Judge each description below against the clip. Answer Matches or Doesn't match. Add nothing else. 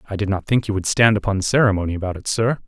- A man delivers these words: Matches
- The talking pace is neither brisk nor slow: Doesn't match